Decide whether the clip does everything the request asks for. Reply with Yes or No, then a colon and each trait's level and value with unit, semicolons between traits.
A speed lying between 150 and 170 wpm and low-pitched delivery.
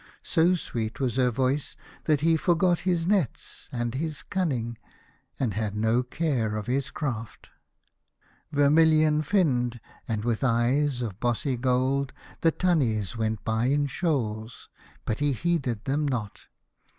No: average, 140 wpm; low, 130 Hz